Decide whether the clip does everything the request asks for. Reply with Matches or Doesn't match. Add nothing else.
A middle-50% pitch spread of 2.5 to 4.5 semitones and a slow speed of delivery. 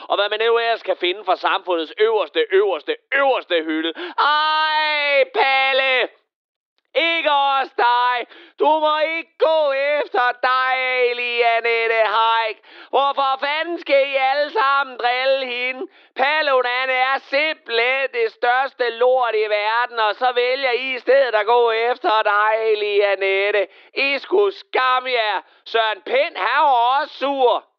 Matches